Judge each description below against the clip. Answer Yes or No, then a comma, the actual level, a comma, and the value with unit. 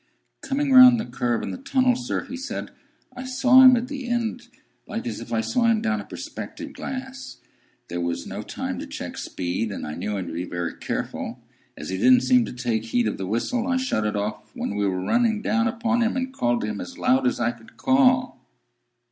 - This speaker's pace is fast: Yes, fast, 225 wpm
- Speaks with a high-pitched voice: Yes, high, 220 Hz